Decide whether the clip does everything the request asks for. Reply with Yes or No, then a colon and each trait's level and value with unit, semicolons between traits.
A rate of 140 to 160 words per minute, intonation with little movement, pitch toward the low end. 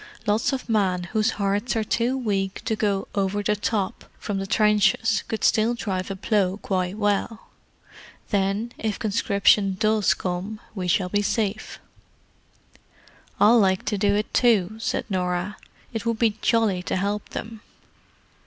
No: average, 150 wpm; narrow, 2.1 semitones; high, 205 Hz